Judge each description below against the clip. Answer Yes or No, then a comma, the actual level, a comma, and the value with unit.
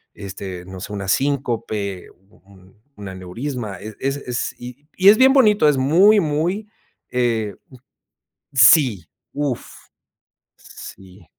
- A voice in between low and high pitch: No, low, 120 Hz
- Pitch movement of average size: No, wide, 7.0 semitones